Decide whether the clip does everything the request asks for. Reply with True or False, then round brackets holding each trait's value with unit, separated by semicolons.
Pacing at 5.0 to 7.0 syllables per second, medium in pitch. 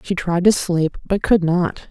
False (4.0 syllables/s; 180 Hz)